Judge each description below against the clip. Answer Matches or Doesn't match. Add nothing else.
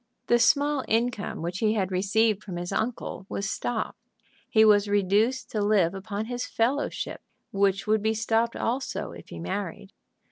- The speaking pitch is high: Matches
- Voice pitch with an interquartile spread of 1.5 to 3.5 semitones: Matches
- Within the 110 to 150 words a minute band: Doesn't match